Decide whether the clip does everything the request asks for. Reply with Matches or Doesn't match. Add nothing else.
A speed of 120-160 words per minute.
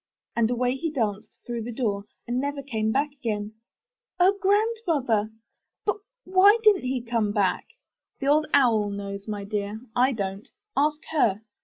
Matches